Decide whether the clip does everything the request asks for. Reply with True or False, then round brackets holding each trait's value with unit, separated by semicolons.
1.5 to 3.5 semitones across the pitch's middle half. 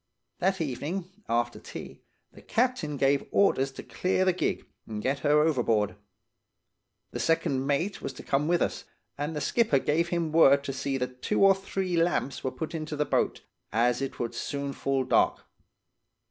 False (4.3 semitones)